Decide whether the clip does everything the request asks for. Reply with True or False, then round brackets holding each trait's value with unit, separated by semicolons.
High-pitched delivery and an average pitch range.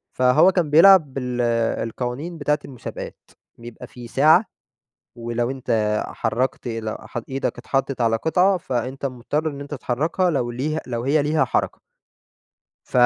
False (135 Hz; 4.3 semitones)